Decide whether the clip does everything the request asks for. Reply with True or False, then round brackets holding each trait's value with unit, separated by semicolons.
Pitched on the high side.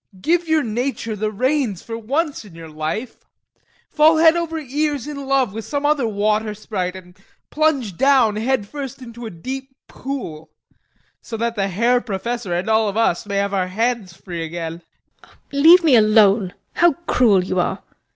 True (225 Hz)